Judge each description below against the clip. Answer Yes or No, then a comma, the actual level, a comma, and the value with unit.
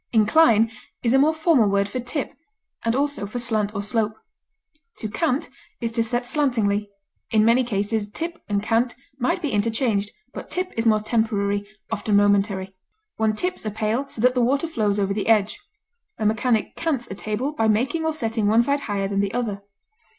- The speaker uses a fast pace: No, average, 185 wpm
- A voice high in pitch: Yes, high, 225 Hz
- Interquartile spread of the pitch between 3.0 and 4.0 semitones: Yes, average, 3.4 semitones